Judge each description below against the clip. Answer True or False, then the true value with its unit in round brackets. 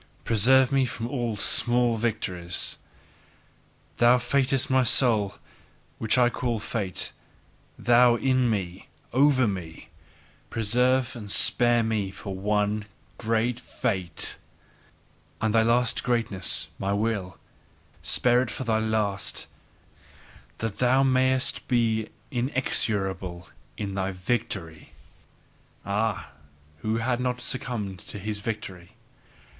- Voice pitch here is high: False (115 Hz)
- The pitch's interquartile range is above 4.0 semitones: False (3.5 semitones)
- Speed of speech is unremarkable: False (110 wpm)